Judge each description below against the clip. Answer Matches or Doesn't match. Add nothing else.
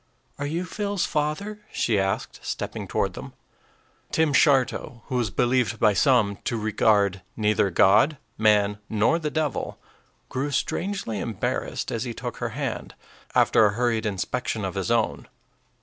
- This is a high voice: Doesn't match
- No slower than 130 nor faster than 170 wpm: Matches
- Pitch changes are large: Matches